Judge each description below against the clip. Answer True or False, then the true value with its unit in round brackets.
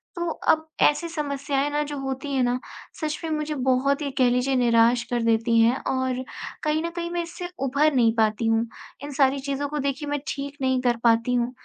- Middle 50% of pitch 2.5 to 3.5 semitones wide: True (3.2 semitones)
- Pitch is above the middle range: True (270 Hz)